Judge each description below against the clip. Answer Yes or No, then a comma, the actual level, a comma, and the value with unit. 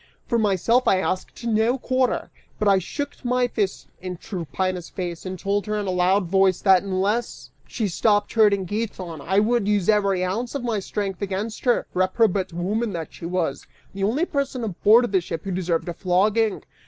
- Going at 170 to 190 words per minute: Yes, average, 185 wpm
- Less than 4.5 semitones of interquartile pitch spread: Yes, average, 3.3 semitones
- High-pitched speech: Yes, high, 200 Hz